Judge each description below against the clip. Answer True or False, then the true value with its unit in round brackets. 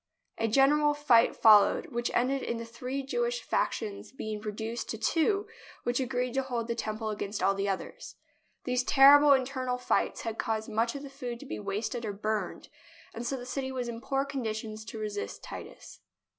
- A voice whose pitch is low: False (240 Hz)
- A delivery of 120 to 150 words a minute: False (195 wpm)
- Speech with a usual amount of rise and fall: True (3.6 semitones)